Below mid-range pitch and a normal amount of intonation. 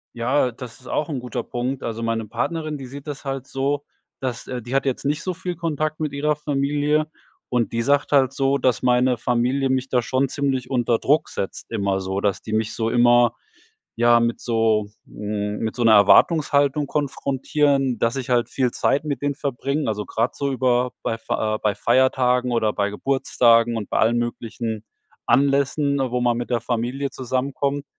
Yes: low, 125 Hz; average, 3.1 semitones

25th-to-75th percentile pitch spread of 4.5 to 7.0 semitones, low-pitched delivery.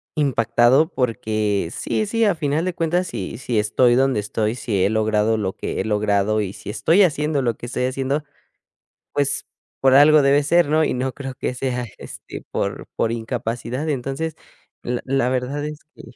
Yes: average, 4.8 semitones; low, 130 Hz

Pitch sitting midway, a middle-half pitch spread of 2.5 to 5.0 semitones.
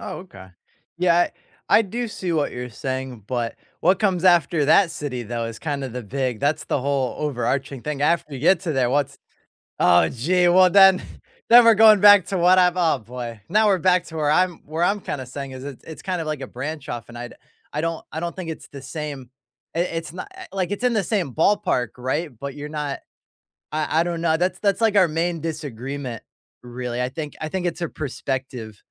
No: medium, 155 Hz; wide, 5.4 semitones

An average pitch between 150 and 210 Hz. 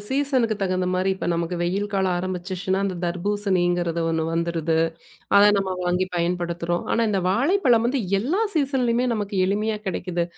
Yes: high, 190 Hz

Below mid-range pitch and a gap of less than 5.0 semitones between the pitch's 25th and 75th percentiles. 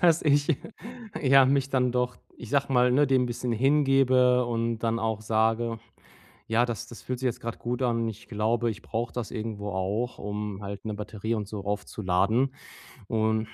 Yes: low, 115 Hz; narrow, 2.6 semitones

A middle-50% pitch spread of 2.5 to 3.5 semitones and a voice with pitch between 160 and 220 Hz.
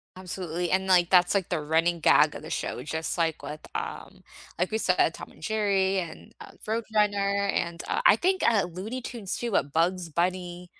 Yes: average, 2.9 semitones; medium, 185 Hz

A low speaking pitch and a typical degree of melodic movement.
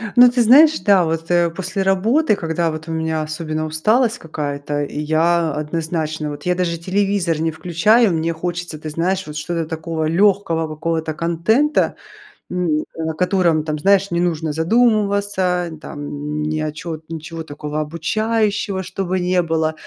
No: medium, 165 Hz; average, 3.3 semitones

